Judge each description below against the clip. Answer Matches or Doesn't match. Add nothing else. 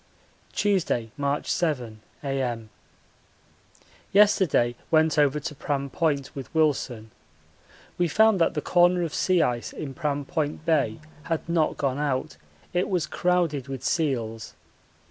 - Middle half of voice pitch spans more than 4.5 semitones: Doesn't match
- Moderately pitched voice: Matches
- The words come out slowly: Matches